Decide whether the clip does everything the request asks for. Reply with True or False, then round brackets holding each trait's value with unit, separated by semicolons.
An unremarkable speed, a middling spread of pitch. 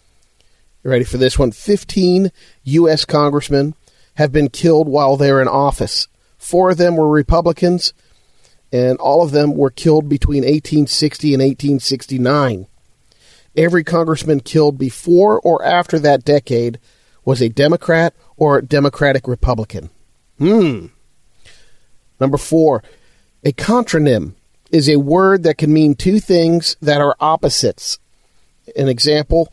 False (125 wpm; 3.5 semitones)